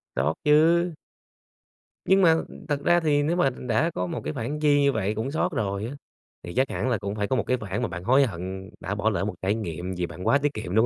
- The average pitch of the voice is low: Yes, low, 115 Hz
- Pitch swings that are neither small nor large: No, wide, 7.2 semitones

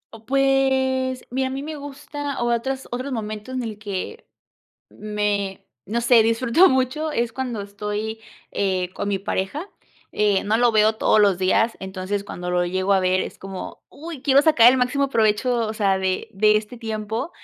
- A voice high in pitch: Yes, high, 225 Hz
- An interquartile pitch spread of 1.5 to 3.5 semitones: No, average, 4.4 semitones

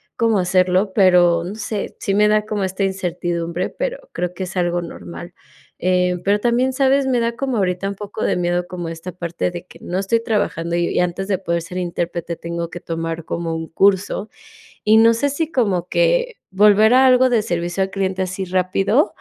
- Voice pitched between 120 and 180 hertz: No, high, 190 Hz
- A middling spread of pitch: Yes, average, 3.7 semitones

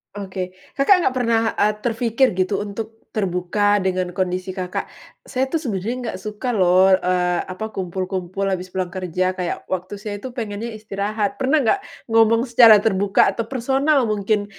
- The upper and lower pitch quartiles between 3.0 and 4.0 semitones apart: Yes, average, 3.6 semitones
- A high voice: Yes, high, 205 Hz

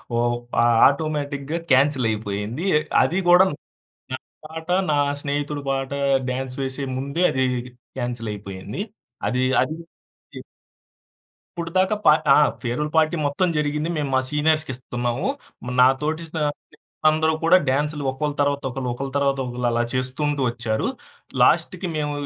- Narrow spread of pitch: No, average, 3.4 semitones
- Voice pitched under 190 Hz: Yes, medium, 140 Hz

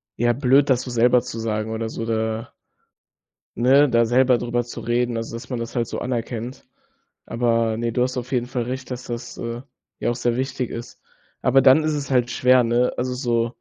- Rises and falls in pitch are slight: Yes, narrow, 1.5 semitones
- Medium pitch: No, low, 120 Hz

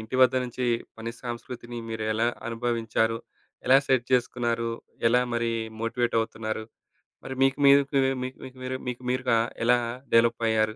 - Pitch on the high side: No, low, 120 Hz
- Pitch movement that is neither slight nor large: No, narrow, 1.8 semitones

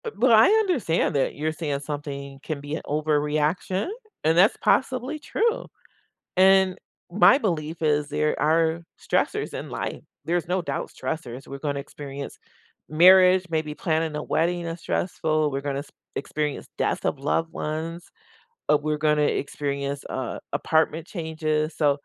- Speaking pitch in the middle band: Yes, medium, 155 Hz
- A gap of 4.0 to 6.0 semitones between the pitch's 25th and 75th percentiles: No, average, 3.0 semitones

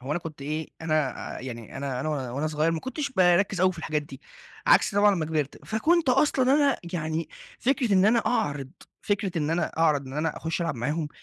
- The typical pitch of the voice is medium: Yes, medium, 165 Hz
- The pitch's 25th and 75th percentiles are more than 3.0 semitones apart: Yes, wide, 5.5 semitones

